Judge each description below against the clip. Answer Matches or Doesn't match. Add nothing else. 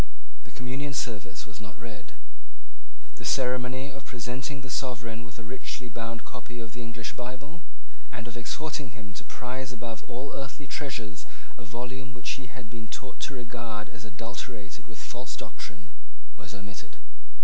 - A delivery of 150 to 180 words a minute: Matches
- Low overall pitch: Matches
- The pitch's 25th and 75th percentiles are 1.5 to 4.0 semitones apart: Matches